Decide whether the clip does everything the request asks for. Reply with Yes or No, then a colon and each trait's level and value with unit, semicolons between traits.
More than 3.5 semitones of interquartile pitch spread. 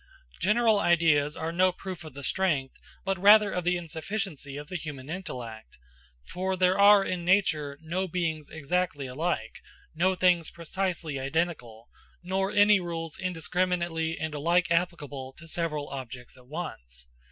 Yes: average, 4.0 semitones